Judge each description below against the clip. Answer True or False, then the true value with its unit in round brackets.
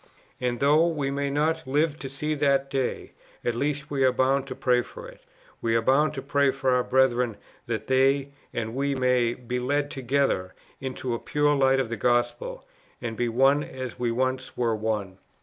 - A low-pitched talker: True (130 Hz)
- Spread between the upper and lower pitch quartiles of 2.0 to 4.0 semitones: True (2.6 semitones)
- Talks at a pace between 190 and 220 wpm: True (195 wpm)